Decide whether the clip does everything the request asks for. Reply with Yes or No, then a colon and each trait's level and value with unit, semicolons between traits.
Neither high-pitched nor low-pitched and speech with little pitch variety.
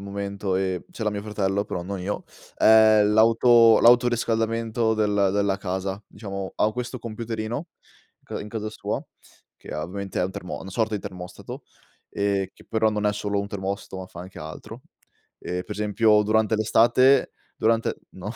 No: low, 105 Hz; narrow, 2.3 semitones